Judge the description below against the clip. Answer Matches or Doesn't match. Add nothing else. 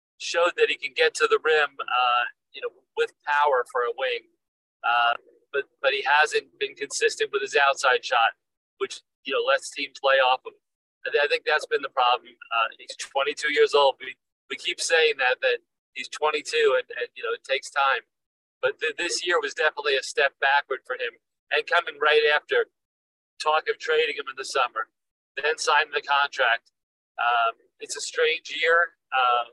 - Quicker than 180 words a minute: Matches